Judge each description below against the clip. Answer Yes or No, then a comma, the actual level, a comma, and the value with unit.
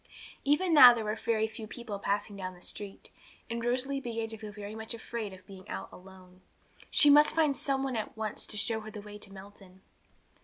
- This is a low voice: No, high, 220 Hz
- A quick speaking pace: Yes, fast, 215 wpm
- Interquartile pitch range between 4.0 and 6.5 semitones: No, average, 3.2 semitones